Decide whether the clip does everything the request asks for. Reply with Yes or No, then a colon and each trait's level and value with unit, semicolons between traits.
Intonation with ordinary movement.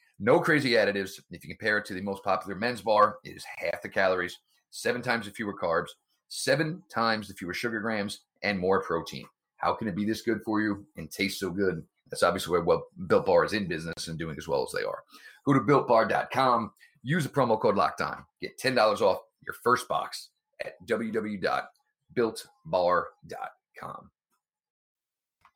No: wide, 8.6 semitones